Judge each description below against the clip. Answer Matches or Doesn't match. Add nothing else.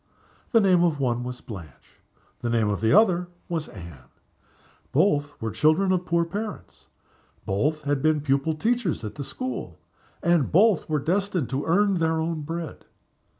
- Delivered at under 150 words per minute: Doesn't match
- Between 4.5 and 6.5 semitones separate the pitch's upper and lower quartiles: Matches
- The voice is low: Doesn't match